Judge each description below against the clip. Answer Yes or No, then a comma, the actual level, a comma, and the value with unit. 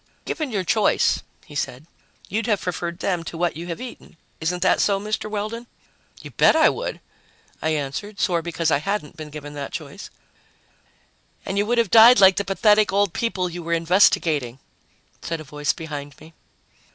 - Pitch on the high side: No, medium, 180 Hz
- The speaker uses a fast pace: No, average, 180 wpm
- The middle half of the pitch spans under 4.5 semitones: No, average, 4.8 semitones